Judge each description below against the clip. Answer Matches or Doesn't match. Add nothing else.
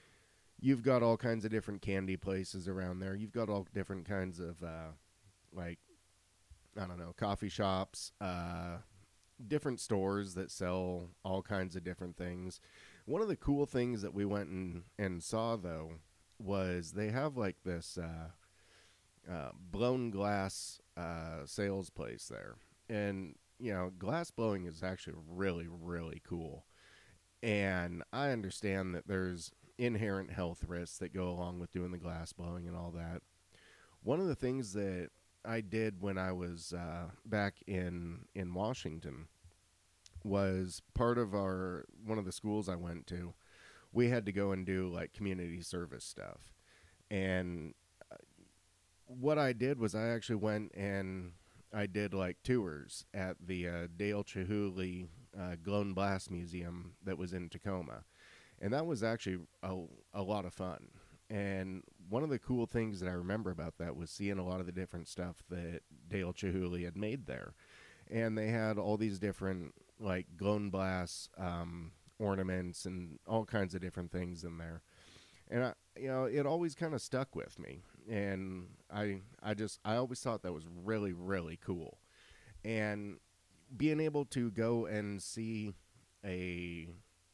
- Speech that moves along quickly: Doesn't match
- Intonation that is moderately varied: Matches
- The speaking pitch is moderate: Doesn't match